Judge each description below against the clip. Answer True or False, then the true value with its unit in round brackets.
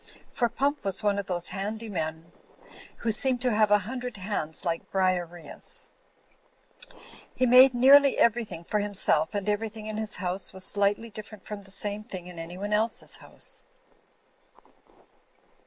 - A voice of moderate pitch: False (205 Hz)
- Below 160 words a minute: True (150 wpm)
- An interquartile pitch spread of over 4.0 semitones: False (3.4 semitones)